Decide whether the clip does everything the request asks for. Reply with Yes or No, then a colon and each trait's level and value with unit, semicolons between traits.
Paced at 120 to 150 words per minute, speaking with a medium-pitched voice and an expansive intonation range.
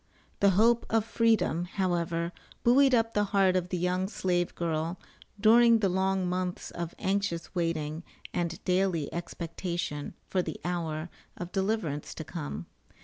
No: average, 145 wpm; medium, 180 Hz; average, 2.9 semitones